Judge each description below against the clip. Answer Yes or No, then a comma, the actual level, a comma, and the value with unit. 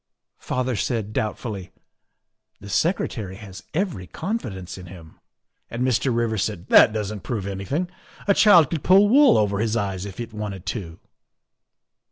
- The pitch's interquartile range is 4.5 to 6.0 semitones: Yes, average, 4.8 semitones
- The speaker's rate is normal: Yes, average, 165 wpm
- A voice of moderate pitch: No, low, 110 Hz